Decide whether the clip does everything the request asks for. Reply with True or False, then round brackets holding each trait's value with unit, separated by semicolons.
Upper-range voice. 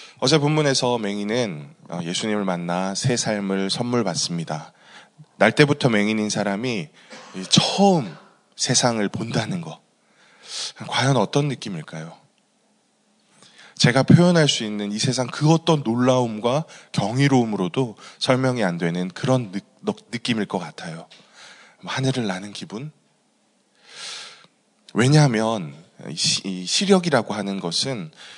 False (120 Hz)